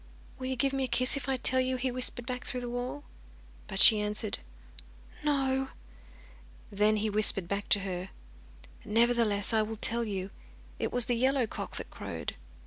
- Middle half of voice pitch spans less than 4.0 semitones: Yes, average, 3.6 semitones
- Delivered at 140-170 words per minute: No, average, 180 wpm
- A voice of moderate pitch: No, high, 235 Hz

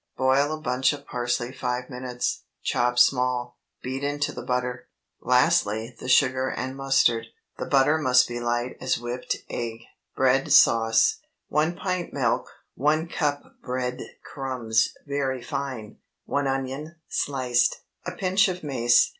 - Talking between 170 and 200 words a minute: No, average, 140 wpm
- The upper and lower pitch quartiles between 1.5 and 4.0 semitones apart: Yes, narrow, 2.6 semitones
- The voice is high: No, low, 130 Hz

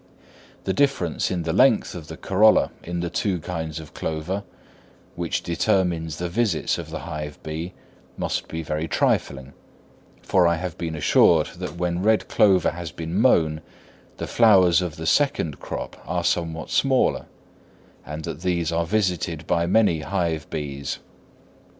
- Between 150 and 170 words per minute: Yes, average, 155 wpm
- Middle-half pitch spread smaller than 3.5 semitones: Yes, average, 2.7 semitones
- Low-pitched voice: Yes, very low, 85 Hz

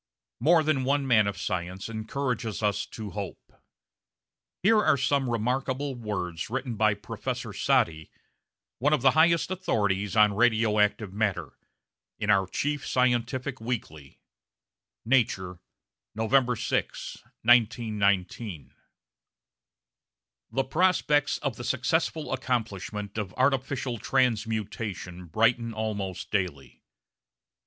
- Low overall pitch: Yes, low, 115 Hz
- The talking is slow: Yes, slow, 105 wpm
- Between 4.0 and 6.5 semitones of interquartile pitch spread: Yes, average, 4.4 semitones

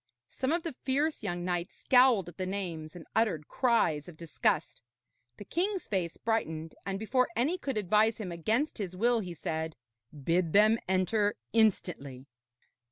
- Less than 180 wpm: Yes, average, 160 wpm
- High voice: Yes, high, 200 Hz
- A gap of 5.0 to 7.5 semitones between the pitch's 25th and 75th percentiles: Yes, average, 5.3 semitones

